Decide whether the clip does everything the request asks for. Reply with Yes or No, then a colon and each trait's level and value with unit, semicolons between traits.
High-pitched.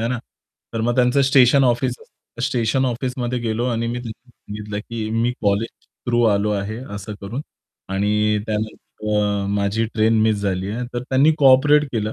No: low, 115 Hz